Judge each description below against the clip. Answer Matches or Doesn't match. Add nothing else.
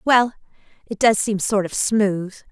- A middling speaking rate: Matches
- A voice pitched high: Matches